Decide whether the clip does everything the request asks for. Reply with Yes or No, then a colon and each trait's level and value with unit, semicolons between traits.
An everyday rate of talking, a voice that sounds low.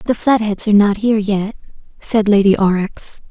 No: average, 165 wpm; high, 210 Hz